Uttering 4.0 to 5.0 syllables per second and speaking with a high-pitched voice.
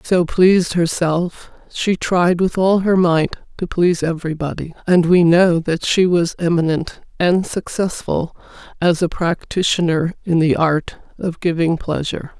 No: 4.3 syllables/s; medium, 170 Hz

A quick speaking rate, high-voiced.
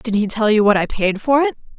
Yes: fast, 305 wpm; high, 225 Hz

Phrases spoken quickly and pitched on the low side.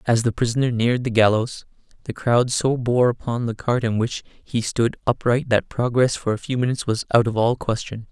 Yes: fast, 215 wpm; low, 120 Hz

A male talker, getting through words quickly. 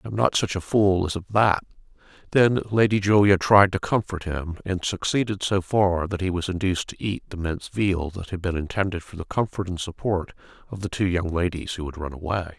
Yes: male; fast, 220 wpm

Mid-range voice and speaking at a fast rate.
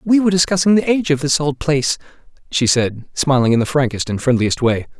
Yes: medium, 145 Hz; fast, 215 wpm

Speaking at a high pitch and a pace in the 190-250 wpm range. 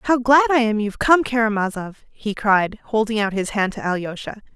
Yes: high, 220 Hz; average, 200 wpm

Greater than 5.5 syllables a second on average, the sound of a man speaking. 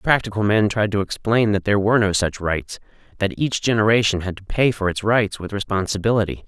Yes: 5.8 syllables/s; male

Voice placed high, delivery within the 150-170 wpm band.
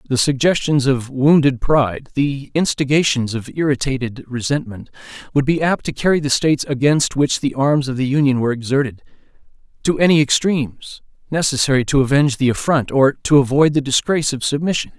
No: medium, 140 Hz; average, 165 wpm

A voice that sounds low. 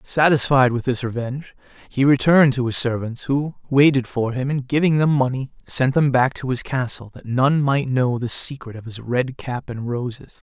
Yes: low, 130 Hz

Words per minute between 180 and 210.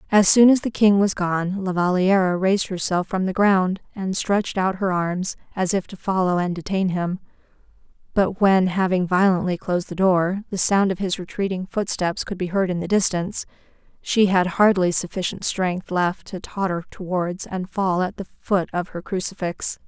Yes: average, 185 wpm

